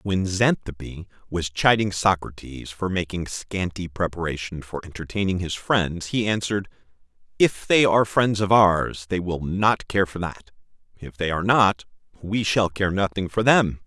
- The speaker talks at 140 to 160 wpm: Yes, average, 155 wpm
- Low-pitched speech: Yes, very low, 95 Hz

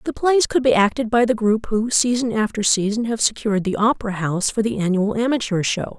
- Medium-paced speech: No, fast, 220 wpm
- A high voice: Yes, high, 220 Hz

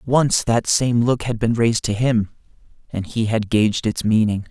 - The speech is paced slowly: No, average, 200 wpm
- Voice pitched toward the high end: No, low, 115 Hz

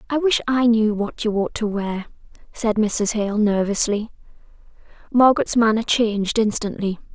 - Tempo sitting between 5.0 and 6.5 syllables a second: No, 4.7 syllables/s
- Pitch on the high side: Yes, high, 220 Hz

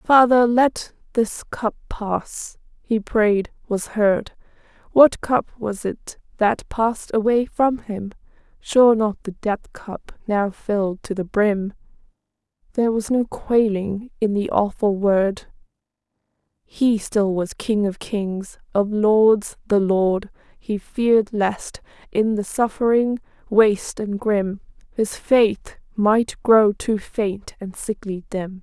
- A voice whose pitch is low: No, high, 215 Hz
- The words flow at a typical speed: No, slow, 130 wpm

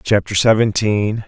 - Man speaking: Yes, male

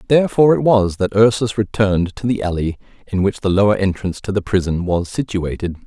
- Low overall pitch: Yes, low, 100 Hz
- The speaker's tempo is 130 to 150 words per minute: No, average, 195 wpm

